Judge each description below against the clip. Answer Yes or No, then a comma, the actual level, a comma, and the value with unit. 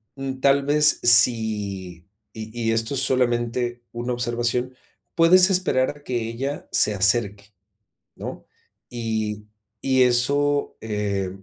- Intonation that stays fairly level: No, average, 3.4 semitones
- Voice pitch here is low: Yes, low, 120 Hz